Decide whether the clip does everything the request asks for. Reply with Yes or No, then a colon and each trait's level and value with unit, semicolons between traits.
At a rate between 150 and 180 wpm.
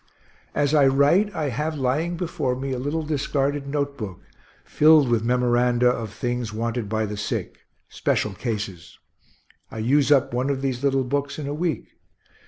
Yes: average, 170 wpm